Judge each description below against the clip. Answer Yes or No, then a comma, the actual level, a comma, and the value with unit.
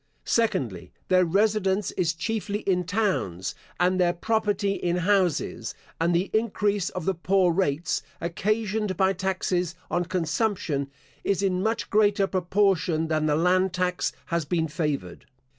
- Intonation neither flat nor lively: Yes, average, 3.0 semitones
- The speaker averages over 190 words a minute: No, average, 140 wpm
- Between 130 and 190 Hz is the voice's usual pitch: Yes, medium, 185 Hz